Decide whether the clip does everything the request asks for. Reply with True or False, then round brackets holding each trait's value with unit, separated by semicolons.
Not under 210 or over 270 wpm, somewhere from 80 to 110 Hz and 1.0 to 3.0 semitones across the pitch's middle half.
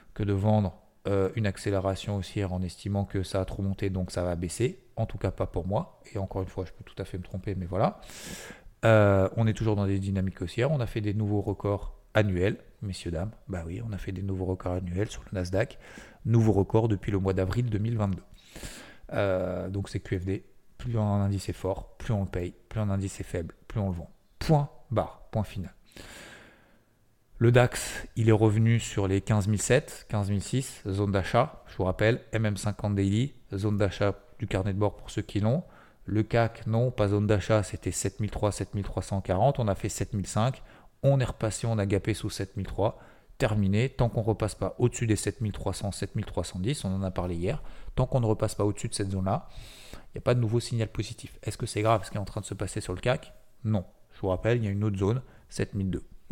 True (220 wpm; 105 Hz; 2.6 semitones)